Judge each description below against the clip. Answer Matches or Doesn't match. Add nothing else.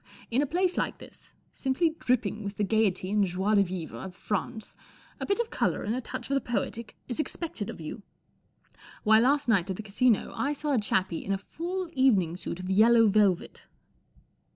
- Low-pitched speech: Doesn't match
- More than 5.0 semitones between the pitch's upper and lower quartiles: Matches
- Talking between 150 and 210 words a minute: Matches